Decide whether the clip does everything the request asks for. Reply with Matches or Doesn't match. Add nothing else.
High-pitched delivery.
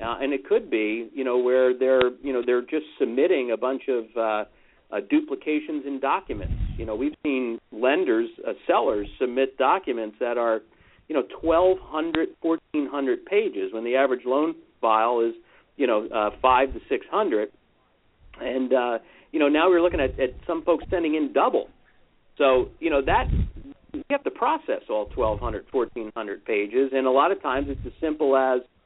Doesn't match